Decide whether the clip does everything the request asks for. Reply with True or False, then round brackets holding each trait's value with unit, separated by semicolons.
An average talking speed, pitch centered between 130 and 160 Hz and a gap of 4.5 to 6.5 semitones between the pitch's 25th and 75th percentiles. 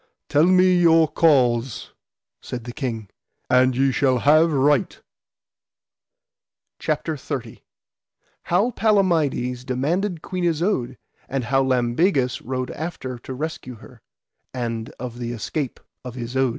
False (120 wpm; 135 Hz; 4.8 semitones)